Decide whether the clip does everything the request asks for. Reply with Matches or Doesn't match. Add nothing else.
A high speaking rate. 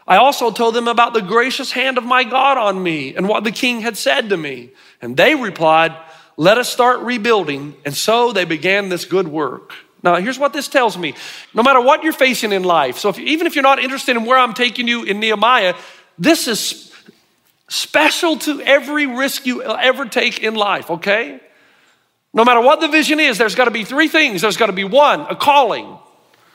Matches